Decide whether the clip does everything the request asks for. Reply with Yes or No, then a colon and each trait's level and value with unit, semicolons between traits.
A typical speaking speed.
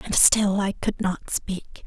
Yes: average, 195 wpm